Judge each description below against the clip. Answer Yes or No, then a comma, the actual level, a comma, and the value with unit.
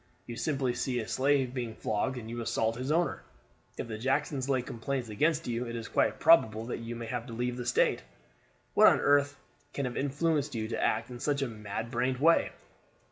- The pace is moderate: No, fast, 210 wpm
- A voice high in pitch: No, low, 125 Hz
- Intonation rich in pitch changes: No, average, 3.2 semitones